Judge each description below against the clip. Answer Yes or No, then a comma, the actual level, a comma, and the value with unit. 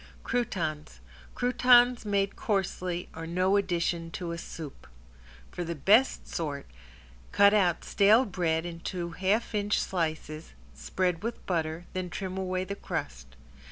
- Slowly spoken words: Yes, slow, 130 wpm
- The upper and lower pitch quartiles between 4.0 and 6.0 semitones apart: No, average, 3.4 semitones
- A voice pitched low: No, medium, 180 Hz